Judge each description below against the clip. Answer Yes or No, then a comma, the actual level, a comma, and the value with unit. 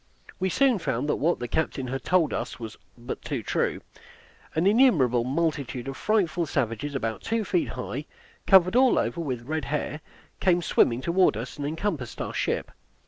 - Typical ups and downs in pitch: No, wide, 6.4 semitones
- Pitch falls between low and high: Yes, medium, 155 Hz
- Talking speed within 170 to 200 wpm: Yes, average, 175 wpm